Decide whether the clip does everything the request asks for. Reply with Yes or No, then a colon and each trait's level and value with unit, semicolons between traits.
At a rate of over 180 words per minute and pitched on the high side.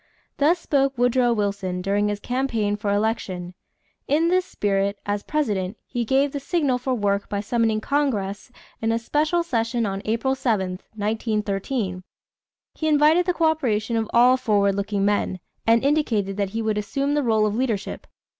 No: average, 165 wpm; high, 225 Hz